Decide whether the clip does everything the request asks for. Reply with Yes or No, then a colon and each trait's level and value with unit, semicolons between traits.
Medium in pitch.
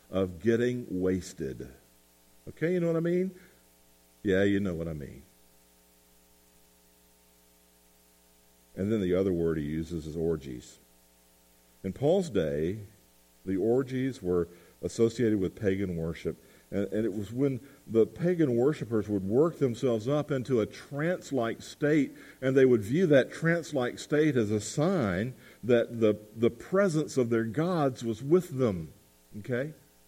No: low, 105 Hz